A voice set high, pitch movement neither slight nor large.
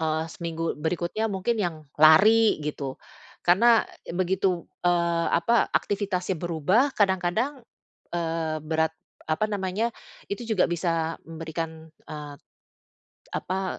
No: medium, 175 Hz; average, 3.9 semitones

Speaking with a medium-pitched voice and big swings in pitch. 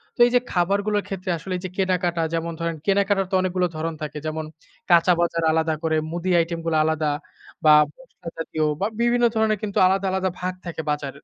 No: medium, 175 Hz; average, 3.0 semitones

